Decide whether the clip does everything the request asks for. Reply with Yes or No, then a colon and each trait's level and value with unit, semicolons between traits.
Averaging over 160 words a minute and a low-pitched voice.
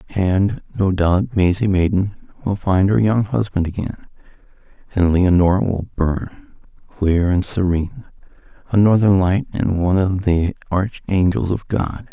No: average, 140 wpm; very low, 95 Hz